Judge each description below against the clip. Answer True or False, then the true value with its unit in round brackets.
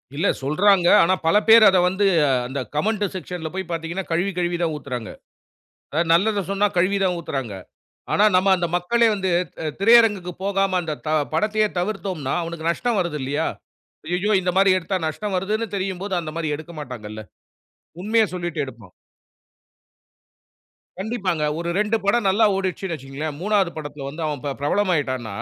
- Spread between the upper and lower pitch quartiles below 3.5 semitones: False (4.3 semitones)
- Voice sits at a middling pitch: True (180 Hz)